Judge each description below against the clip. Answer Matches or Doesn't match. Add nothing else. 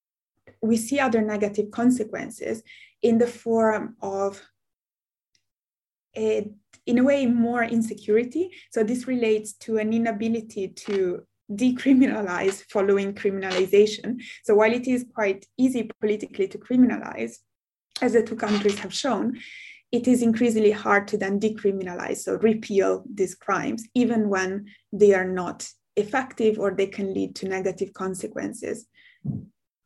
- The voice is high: Matches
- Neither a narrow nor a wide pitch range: Matches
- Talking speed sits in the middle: Doesn't match